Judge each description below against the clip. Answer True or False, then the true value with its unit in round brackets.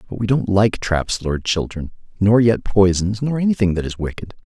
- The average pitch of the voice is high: False (100 Hz)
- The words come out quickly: False (190 wpm)